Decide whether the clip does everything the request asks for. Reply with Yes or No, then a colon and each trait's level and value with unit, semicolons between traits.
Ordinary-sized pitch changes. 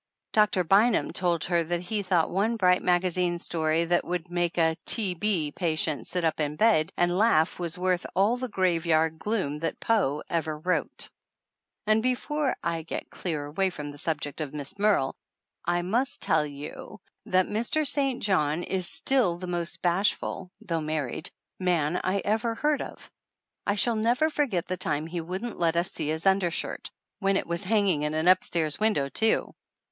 Yes: average, 4.1 semitones